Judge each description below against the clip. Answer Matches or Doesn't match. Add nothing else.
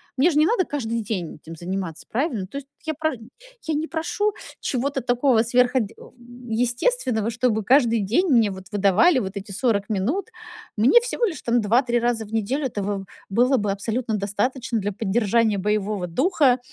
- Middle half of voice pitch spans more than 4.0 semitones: Matches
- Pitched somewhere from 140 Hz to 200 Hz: Doesn't match